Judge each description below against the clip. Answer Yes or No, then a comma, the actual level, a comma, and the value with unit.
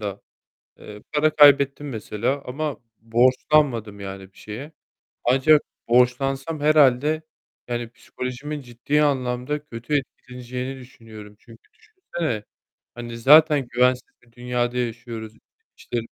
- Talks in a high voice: No, low, 125 Hz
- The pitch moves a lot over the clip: No, average, 3.6 semitones